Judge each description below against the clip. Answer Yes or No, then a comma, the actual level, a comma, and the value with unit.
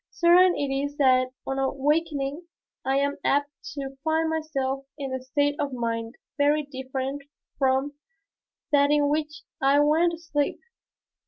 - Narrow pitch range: Yes, narrow, 2.0 semitones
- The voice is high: Yes, very high, 285 Hz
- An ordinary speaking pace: Yes, average, 145 wpm